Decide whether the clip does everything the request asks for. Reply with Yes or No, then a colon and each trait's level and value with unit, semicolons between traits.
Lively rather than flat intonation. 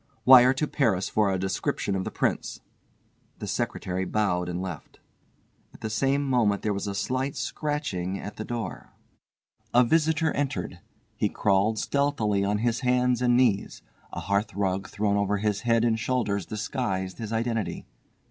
No: average, 4.2 semitones